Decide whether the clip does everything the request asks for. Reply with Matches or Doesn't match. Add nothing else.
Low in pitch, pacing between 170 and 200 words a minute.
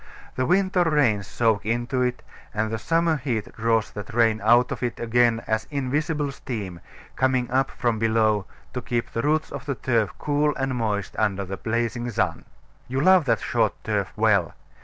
Matches